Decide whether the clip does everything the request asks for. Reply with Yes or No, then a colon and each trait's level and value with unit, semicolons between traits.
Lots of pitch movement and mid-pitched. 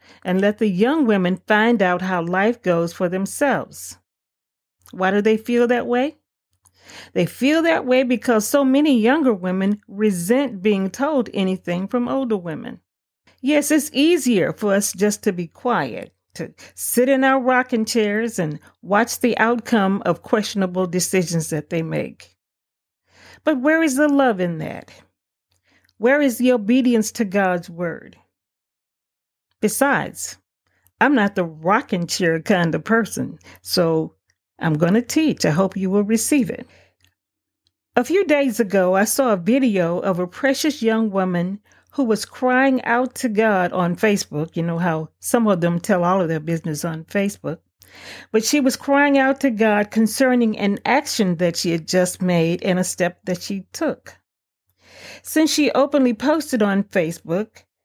No: wide, 5.9 semitones; high, 210 Hz